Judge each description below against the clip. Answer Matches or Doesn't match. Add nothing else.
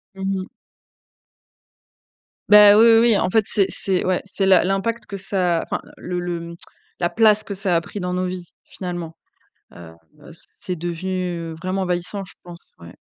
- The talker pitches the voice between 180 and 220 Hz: Matches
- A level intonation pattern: Matches